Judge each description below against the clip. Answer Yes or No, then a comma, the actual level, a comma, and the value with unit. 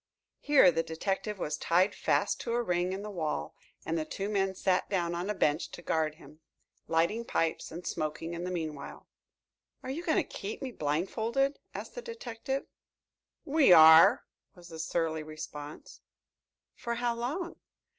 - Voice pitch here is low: No, medium, 180 Hz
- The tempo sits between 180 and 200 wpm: No, average, 165 wpm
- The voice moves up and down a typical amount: No, wide, 6.4 semitones